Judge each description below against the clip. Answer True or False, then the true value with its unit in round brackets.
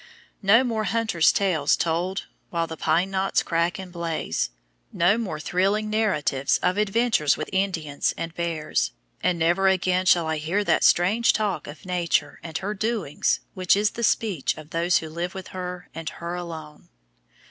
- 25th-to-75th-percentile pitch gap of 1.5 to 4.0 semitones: True (3.2 semitones)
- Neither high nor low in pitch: True (180 Hz)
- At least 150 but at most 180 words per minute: True (170 wpm)